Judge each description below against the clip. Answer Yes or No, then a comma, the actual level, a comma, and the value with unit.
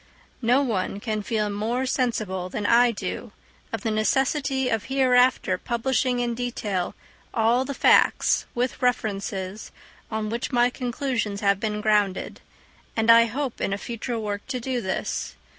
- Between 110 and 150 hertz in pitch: No, high, 230 Hz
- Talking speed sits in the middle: Yes, average, 150 wpm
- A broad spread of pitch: No, average, 3.1 semitones